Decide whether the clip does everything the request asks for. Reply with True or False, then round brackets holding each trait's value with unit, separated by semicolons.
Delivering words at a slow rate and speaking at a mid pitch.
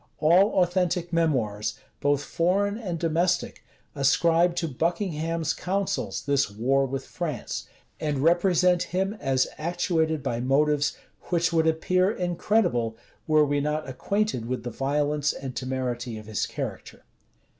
True (130 wpm; 155 Hz)